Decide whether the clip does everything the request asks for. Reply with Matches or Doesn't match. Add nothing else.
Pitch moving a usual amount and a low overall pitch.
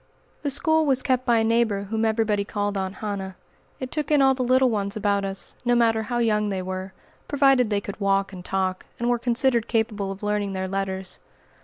Doesn't match